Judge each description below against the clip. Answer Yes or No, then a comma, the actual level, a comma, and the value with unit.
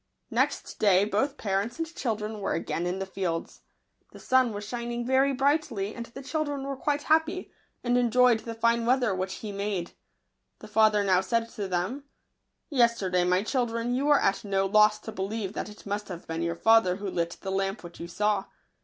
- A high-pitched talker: Yes, high, 215 Hz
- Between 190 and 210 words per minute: Yes, average, 200 wpm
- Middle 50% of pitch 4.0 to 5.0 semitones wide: Yes, average, 4.3 semitones